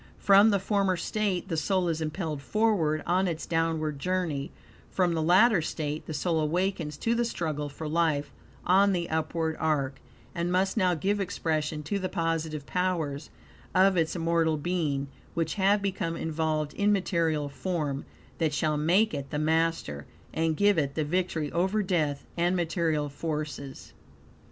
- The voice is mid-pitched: Yes, medium, 165 Hz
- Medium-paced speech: Yes, average, 160 wpm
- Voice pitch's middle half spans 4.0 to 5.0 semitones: No, average, 3.3 semitones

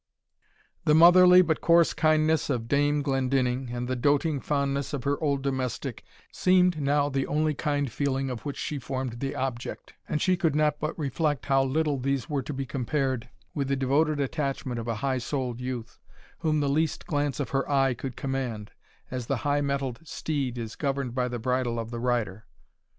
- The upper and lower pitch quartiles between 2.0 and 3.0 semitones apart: Yes, average, 2.7 semitones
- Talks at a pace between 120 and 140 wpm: No, average, 190 wpm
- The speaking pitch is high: No, medium, 140 Hz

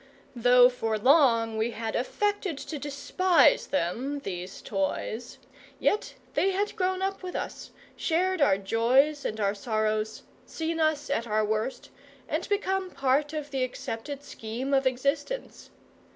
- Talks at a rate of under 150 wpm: Yes, average, 140 wpm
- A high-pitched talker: Yes, very high, 270 Hz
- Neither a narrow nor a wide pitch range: No, wide, 6.2 semitones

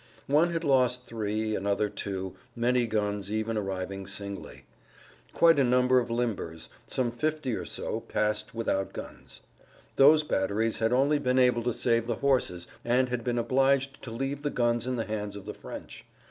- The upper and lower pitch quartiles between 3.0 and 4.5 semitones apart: Yes, average, 3.5 semitones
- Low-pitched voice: Yes, low, 120 Hz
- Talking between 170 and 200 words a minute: Yes, average, 175 wpm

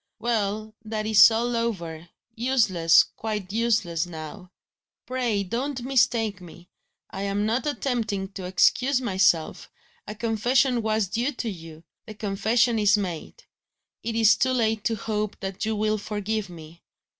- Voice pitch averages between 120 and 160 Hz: No, high, 215 Hz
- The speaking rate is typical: Yes, average, 145 wpm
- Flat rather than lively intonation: No, average, 3.3 semitones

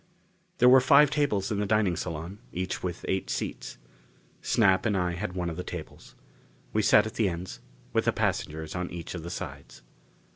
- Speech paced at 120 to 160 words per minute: No, average, 190 wpm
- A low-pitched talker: Yes, very low, 95 Hz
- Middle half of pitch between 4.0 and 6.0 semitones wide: No, average, 3.6 semitones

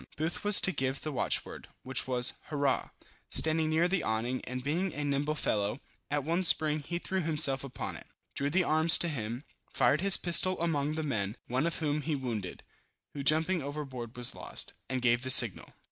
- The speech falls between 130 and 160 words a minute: No, average, 190 wpm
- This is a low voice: No, medium, 145 Hz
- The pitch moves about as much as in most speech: Yes, average, 3.9 semitones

